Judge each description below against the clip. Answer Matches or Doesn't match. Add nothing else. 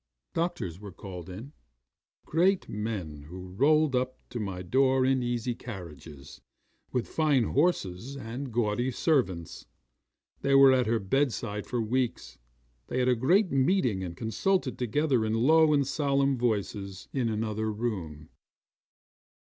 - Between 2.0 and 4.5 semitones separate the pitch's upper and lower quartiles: Doesn't match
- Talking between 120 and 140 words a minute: Matches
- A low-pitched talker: Matches